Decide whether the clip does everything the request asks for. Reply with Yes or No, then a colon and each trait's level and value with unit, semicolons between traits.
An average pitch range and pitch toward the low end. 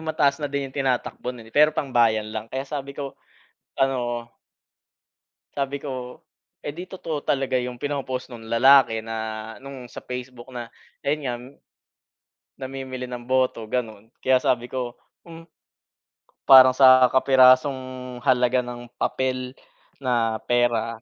No: narrow, 1.9 semitones; low, 130 Hz